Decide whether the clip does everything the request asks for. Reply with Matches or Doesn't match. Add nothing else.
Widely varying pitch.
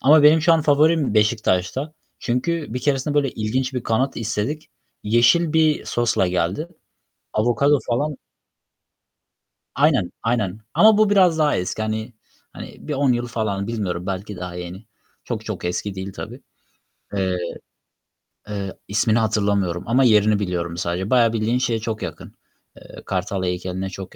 Matches